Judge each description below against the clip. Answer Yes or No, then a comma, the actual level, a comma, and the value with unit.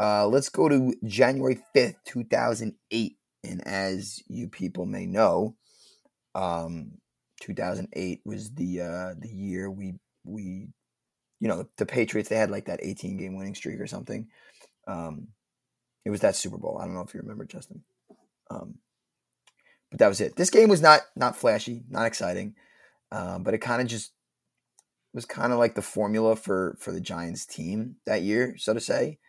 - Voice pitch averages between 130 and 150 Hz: No, low, 105 Hz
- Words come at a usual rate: Yes, average, 175 wpm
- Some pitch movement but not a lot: Yes, average, 4.2 semitones